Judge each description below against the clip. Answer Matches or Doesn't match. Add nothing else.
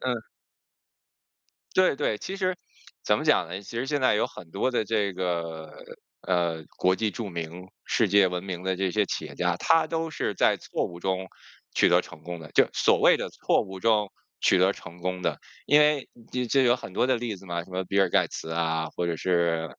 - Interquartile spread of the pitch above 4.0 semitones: Matches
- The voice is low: Matches